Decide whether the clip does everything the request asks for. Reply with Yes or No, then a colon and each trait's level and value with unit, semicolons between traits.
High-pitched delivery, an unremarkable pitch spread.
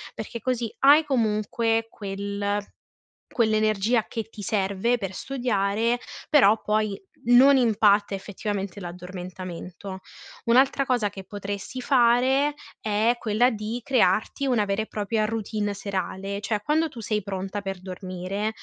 Yes: high, 215 Hz; average, 3.1 semitones